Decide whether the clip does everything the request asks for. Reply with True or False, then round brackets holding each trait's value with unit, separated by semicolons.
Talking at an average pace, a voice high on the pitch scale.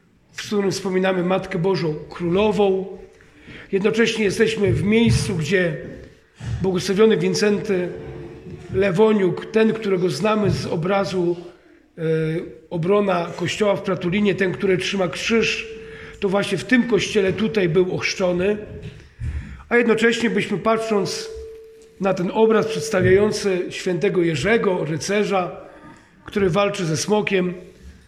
False (105 wpm; 195 Hz)